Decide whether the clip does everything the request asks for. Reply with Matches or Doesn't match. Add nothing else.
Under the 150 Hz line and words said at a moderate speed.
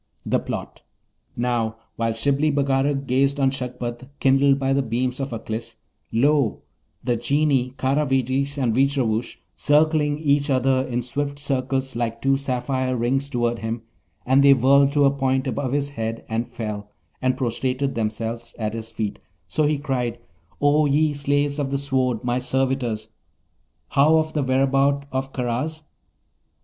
Matches